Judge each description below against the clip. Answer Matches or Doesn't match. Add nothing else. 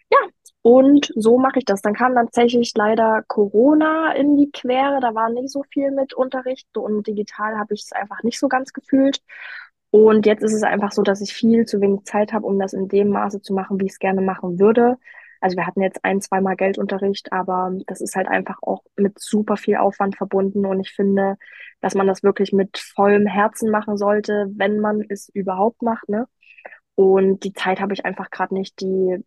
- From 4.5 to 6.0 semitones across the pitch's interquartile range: Doesn't match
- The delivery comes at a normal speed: Doesn't match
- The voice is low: Doesn't match